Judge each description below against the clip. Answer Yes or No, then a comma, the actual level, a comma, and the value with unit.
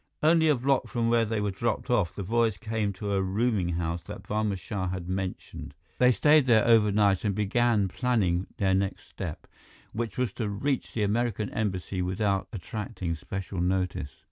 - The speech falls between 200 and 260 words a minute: No, average, 175 wpm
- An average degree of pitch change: Yes, average, 3.7 semitones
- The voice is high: No, low, 105 Hz